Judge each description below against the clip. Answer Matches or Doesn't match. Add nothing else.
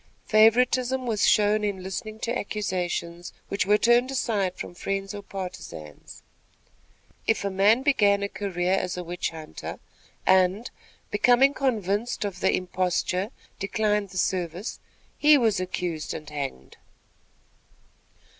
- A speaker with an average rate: Doesn't match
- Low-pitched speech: Doesn't match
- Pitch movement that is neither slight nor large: Matches